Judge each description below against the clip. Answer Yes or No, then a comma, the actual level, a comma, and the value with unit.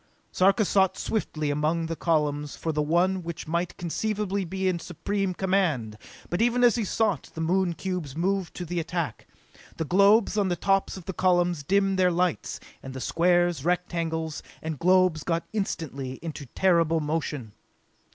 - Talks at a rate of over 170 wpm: No, average, 165 wpm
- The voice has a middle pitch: Yes, medium, 175 Hz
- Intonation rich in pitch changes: No, average, 3.0 semitones